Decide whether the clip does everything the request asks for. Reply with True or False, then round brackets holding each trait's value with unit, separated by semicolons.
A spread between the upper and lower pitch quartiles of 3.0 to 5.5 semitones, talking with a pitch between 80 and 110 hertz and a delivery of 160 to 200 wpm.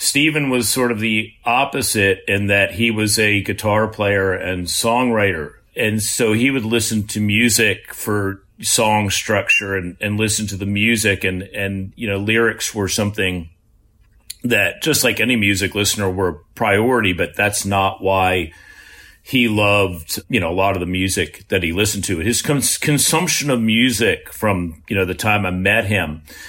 False (2.4 semitones; 105 Hz; 170 wpm)